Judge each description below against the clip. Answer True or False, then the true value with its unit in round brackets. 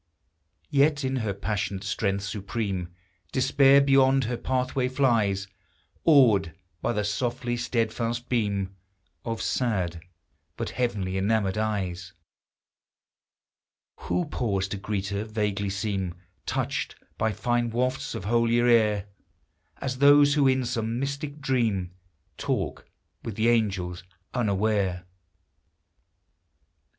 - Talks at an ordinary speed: False (110 wpm)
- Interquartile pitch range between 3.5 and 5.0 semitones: True (4.4 semitones)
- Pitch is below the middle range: True (115 Hz)